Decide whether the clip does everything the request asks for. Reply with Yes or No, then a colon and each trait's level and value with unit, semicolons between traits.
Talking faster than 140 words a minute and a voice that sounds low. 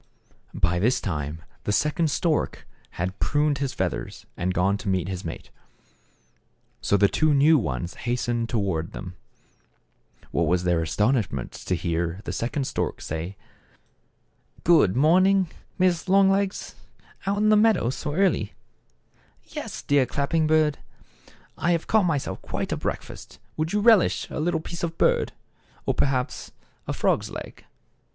Yes: average, 155 wpm; low, 130 Hz